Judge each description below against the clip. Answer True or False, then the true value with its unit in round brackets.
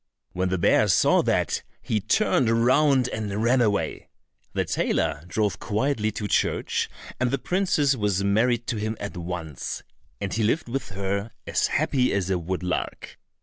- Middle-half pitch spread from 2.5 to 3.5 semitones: False (4.4 semitones)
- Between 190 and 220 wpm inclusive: False (160 wpm)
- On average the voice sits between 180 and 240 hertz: False (110 Hz)